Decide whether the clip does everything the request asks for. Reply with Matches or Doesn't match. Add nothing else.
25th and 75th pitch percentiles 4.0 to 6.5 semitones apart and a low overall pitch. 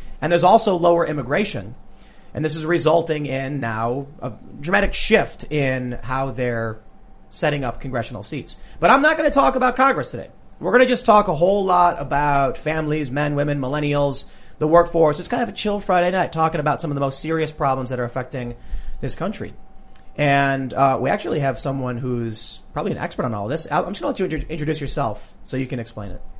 Doesn't match